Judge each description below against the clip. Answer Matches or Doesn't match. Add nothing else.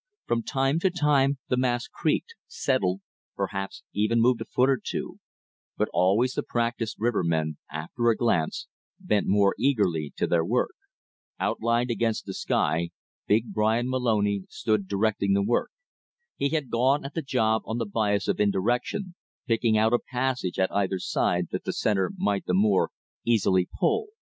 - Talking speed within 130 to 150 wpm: Doesn't match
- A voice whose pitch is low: Matches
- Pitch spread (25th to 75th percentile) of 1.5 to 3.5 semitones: Doesn't match